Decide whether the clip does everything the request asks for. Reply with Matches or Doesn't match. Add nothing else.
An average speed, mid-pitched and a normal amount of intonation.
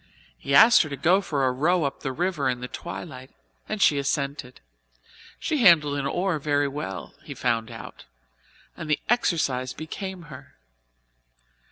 Matches